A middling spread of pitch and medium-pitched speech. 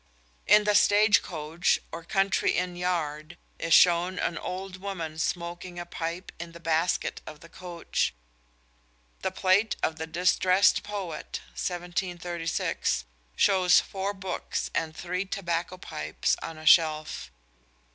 No: narrow, 2.2 semitones; medium, 175 Hz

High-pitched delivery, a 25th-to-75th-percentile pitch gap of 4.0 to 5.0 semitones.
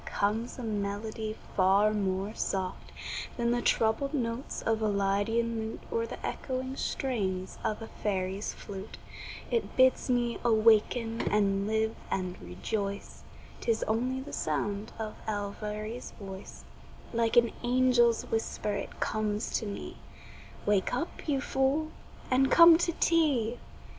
No: high, 220 Hz; average, 3.2 semitones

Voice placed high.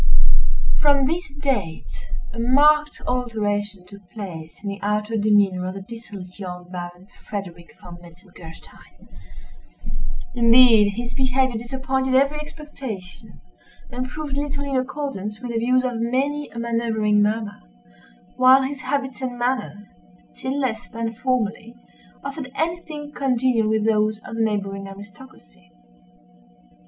Yes: high, 230 Hz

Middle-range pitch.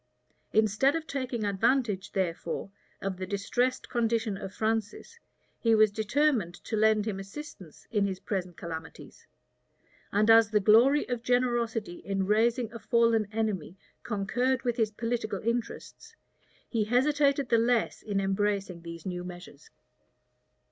No: high, 220 Hz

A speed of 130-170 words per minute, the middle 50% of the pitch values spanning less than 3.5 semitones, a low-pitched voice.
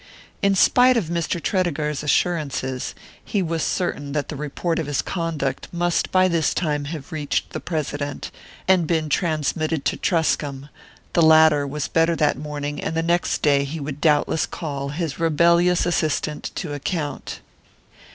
No: average, 155 wpm; average, 2.8 semitones; medium, 155 Hz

